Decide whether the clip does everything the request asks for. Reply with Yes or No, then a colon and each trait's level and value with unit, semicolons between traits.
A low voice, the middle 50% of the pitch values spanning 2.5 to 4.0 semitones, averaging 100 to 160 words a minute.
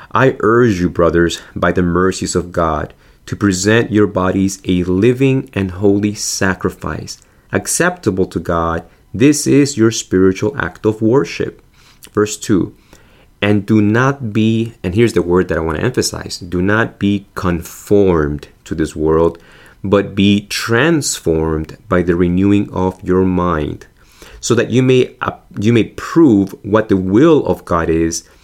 Yes: very low, 95 Hz; average, 3.5 semitones; average, 155 wpm